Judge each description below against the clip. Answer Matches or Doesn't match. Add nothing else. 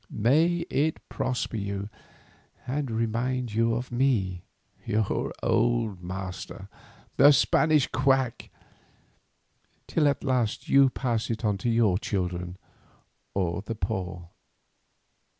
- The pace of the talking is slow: Matches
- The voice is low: Matches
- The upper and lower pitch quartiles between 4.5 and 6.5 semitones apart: Matches